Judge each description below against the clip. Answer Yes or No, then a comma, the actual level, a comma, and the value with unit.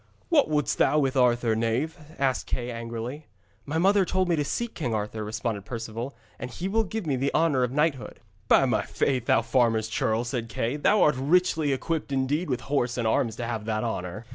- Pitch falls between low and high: No, low, 130 Hz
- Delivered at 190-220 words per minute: Yes, fast, 205 wpm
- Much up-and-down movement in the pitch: No, average, 4.9 semitones